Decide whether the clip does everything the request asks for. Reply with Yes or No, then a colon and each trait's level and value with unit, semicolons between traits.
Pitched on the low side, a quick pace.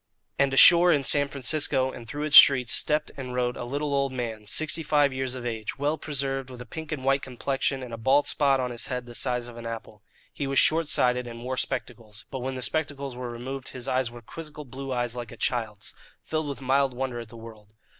Yes: low, 130 Hz; fast, 230 wpm